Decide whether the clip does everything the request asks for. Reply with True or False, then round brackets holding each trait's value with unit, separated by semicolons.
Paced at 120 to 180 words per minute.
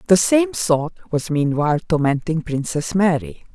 True (135 wpm)